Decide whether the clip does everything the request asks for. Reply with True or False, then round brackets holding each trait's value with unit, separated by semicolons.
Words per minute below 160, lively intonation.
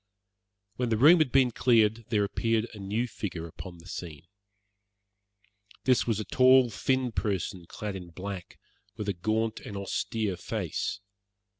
False (150 wpm; 3.7 semitones)